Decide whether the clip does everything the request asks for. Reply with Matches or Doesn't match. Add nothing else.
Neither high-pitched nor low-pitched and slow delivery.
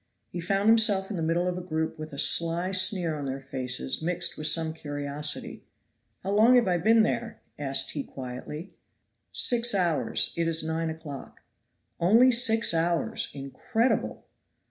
Doesn't match